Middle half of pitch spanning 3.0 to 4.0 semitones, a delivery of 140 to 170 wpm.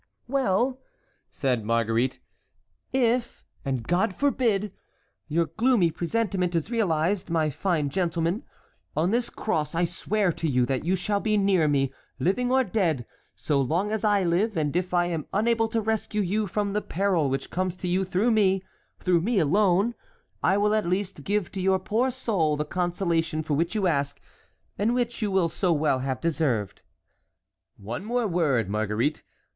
No: average, 5.2 semitones; average, 165 wpm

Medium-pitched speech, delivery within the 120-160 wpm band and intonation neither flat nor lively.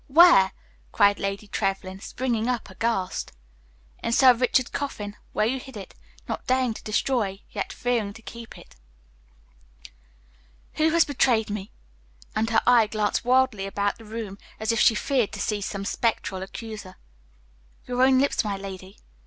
No: high, 220 Hz; average, 155 wpm; average, 3.8 semitones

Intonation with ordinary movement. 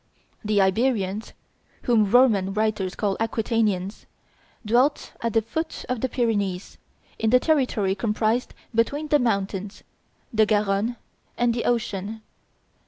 Yes: average, 3.1 semitones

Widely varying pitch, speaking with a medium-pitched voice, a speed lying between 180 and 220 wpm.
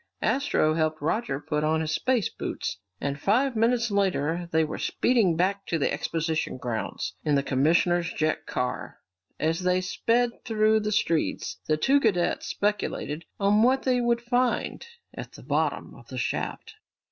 No: wide, 6.6 semitones; medium, 180 Hz; average, 160 wpm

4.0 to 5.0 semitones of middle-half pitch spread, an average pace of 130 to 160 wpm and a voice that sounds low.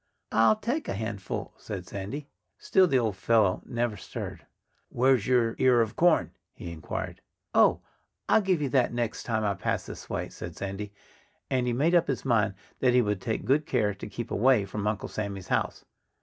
No: average, 4.4 semitones; average, 190 wpm; low, 115 Hz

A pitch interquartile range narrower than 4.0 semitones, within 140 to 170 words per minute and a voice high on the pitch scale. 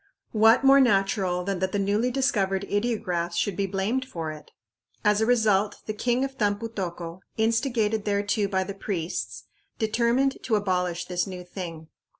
Yes: average, 3.6 semitones; average, 160 wpm; high, 205 Hz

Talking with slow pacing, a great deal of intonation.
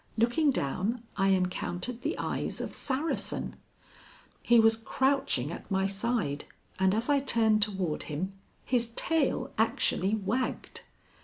No: slow, 130 wpm; average, 4.7 semitones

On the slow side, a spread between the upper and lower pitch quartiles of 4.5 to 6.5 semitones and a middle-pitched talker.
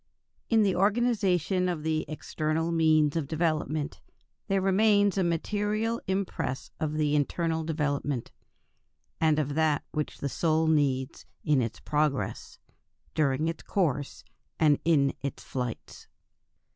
No: slow, 125 wpm; average, 3.7 semitones; medium, 155 Hz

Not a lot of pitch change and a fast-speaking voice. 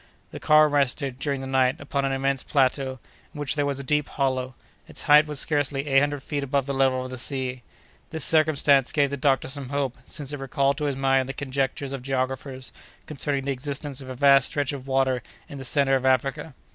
Yes: narrow, 1.5 semitones; fast, 220 wpm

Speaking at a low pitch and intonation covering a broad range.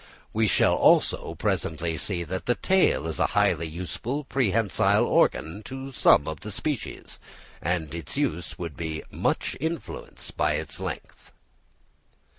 Yes: very low, 90 Hz; wide, 8.3 semitones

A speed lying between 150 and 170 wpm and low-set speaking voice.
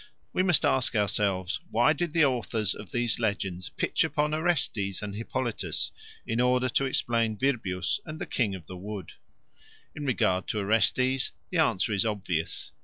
Yes: average, 165 wpm; low, 115 Hz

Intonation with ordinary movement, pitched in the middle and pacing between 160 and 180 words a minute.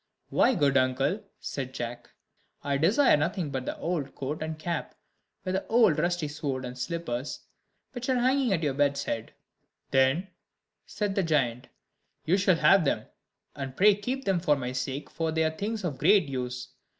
No: wide, 6.1 semitones; medium, 155 Hz; average, 175 wpm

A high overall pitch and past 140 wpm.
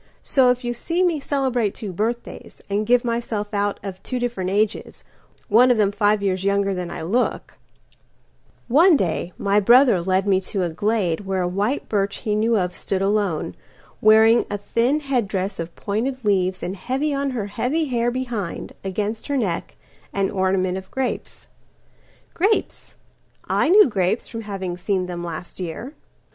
Yes: high, 210 Hz; average, 155 wpm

